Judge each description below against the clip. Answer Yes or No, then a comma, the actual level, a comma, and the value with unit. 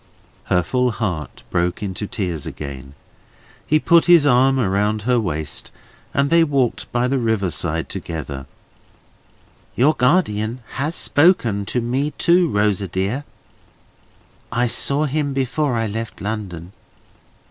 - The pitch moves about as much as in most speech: No, wide, 6.5 semitones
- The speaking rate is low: Yes, slow, 130 wpm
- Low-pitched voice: Yes, low, 115 Hz